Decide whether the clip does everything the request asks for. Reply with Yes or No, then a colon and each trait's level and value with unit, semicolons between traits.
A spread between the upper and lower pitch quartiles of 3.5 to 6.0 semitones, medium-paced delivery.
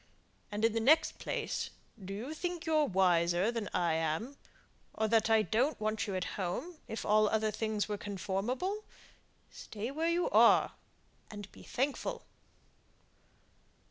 Yes: wide, 5.5 semitones; average, 145 wpm